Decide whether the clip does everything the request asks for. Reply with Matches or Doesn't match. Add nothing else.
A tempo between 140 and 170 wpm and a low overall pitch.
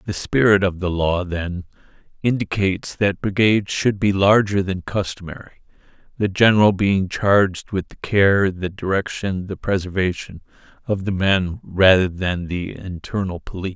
Matches